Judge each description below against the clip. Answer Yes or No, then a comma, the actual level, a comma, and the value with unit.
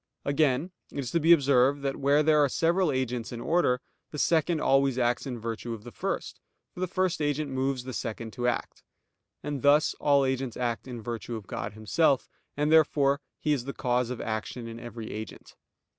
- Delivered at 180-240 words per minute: Yes, average, 200 wpm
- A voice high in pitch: No, low, 135 Hz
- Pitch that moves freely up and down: No, average, 3.6 semitones